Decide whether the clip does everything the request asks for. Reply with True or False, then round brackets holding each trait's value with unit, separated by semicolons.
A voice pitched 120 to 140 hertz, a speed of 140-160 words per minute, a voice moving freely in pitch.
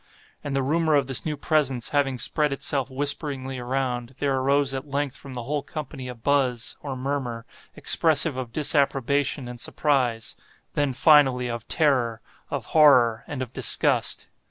False (135 Hz; 155 wpm; 2.4 semitones)